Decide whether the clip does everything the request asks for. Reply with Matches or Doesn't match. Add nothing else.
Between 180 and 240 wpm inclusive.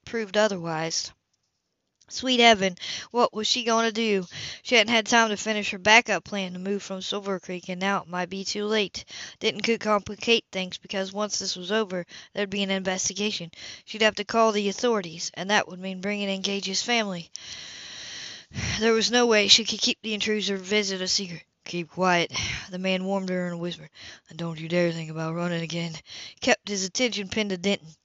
Matches